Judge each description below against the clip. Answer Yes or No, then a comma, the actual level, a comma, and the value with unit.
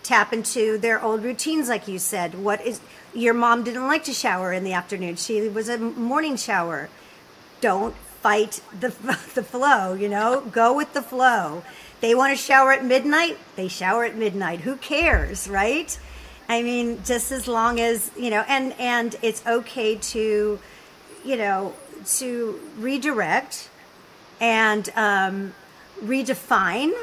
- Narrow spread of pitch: No, average, 3.5 semitones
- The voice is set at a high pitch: Yes, high, 230 Hz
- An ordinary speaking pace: Yes, average, 150 wpm